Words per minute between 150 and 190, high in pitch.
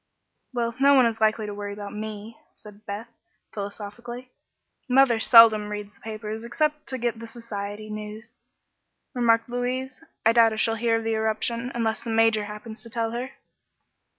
Yes: average, 170 wpm; high, 225 Hz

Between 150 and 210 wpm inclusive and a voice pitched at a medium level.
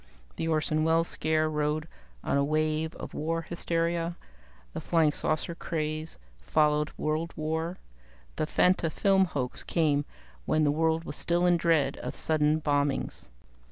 No: average, 140 wpm; medium, 155 Hz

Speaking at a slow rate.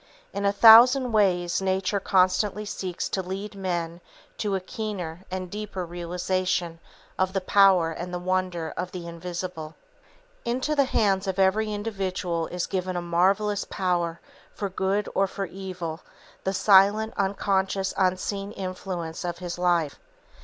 No: average, 145 wpm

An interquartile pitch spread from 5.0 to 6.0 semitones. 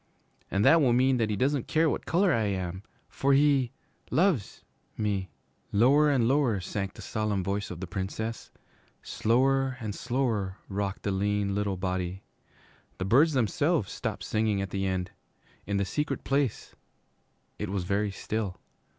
Yes: average, 5.3 semitones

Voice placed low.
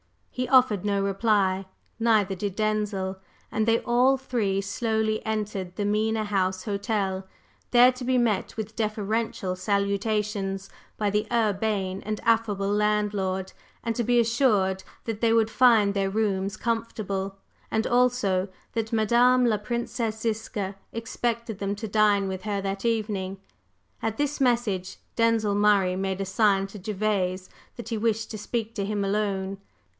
No: high, 210 Hz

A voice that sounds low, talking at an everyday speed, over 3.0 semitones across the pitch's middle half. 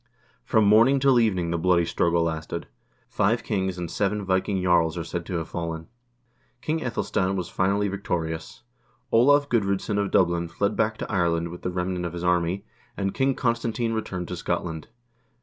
Yes: very low, 95 Hz; average, 170 wpm; average, 3.8 semitones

